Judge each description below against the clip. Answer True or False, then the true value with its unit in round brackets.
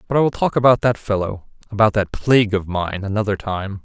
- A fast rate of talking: True (220 wpm)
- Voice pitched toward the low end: True (105 Hz)